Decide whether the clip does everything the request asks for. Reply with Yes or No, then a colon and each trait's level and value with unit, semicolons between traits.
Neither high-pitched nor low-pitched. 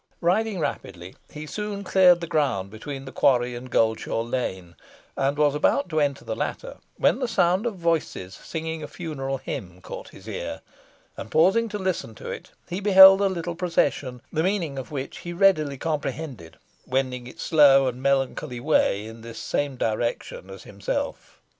Yes: medium, 145 Hz